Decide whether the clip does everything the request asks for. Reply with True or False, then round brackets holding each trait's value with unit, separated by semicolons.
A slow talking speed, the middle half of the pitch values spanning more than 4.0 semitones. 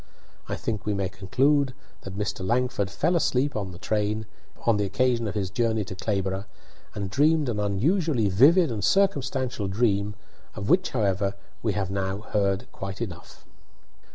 False (160 wpm; 4.7 semitones)